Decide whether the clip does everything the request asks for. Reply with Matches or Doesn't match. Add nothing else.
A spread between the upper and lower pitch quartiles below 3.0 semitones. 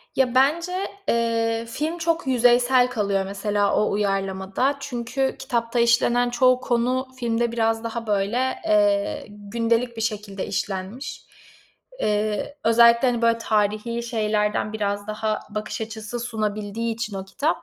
Matches